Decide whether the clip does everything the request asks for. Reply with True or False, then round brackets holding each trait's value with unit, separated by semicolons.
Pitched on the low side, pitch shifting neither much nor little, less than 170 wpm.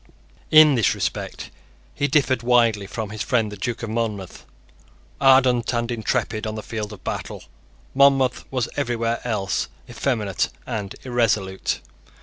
True (115 Hz; 3.0 semitones; 135 wpm)